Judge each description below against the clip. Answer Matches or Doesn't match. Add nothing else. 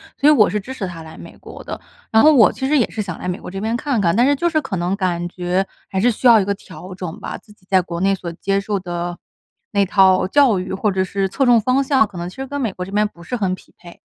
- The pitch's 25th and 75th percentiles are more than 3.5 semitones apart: Matches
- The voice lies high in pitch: Matches